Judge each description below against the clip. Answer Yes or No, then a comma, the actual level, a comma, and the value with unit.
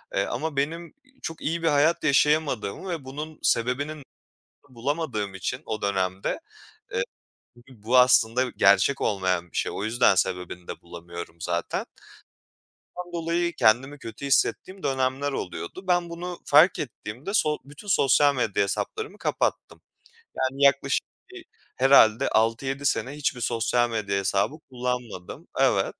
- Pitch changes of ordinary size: No, wide, 6.3 semitones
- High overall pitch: No, low, 130 Hz